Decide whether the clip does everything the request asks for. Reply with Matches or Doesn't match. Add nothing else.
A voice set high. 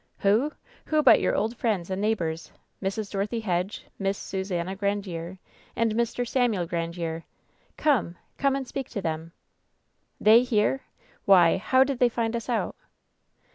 Matches